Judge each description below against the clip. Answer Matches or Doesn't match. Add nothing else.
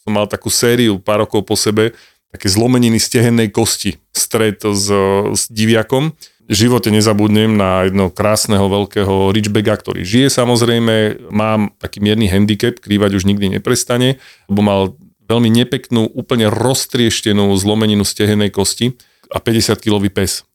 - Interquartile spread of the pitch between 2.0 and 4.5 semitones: Matches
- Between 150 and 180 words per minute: Doesn't match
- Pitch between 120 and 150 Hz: Doesn't match